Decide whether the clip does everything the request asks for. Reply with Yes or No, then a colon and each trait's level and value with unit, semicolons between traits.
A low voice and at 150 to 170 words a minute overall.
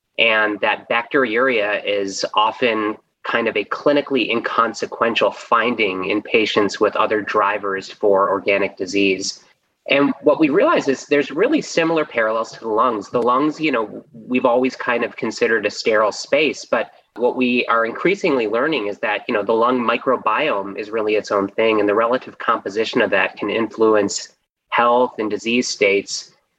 Yes: low, 110 Hz; average, 165 wpm